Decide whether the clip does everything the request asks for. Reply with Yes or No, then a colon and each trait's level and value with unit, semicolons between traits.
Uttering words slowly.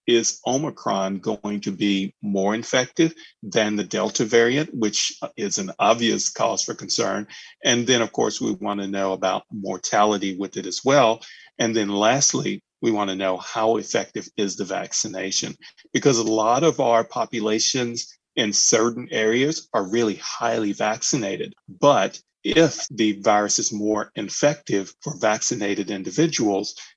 No: average, 150 wpm